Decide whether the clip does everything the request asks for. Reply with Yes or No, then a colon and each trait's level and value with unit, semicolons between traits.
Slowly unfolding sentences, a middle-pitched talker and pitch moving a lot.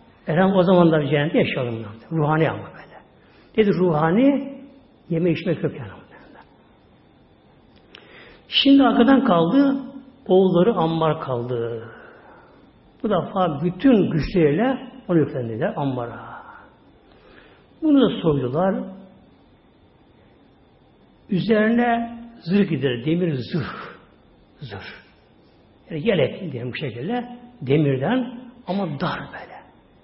Yes: slow, 90 wpm; medium, 180 Hz; wide, 8.4 semitones